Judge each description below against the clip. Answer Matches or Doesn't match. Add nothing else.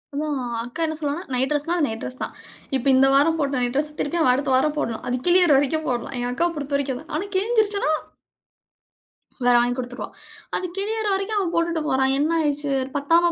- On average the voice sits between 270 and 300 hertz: Matches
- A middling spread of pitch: Matches